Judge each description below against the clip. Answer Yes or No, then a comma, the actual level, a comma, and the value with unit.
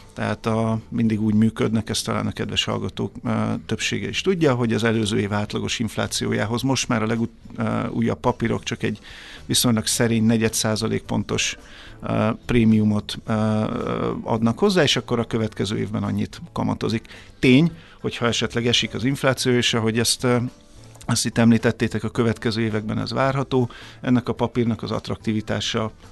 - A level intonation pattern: Yes, narrow, 1.8 semitones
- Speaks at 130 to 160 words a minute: Yes, average, 145 wpm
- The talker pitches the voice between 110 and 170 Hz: Yes, low, 115 Hz